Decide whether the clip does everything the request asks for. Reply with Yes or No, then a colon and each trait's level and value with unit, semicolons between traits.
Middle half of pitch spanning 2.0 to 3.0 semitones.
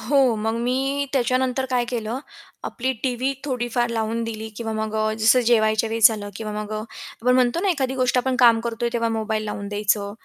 Yes: average, 2.7 semitones